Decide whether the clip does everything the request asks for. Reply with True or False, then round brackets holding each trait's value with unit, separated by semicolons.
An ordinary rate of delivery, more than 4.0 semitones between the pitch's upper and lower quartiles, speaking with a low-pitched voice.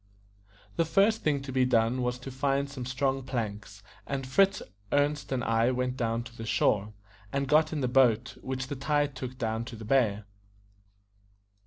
False (180 wpm; 3.1 semitones; 130 Hz)